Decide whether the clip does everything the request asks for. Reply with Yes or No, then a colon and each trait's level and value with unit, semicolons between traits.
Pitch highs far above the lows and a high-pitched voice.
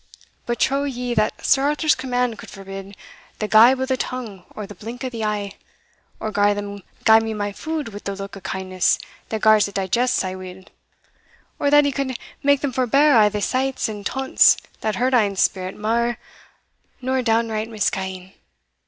No: average, 4.2 semitones; high, 220 Hz